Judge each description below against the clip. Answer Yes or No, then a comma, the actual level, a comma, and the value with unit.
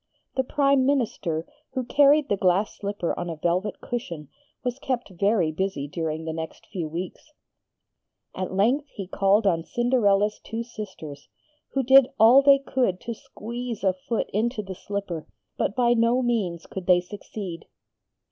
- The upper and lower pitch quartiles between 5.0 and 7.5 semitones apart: Yes, wide, 5.4 semitones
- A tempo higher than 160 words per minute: No, average, 155 wpm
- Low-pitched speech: No, high, 205 Hz